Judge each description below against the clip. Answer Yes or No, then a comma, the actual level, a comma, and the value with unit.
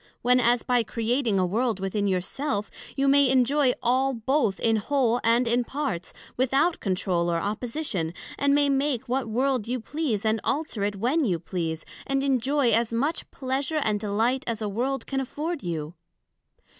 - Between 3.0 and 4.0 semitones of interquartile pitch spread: No, average, 4.7 semitones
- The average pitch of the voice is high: Yes, high, 245 Hz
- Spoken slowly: No, average, 175 wpm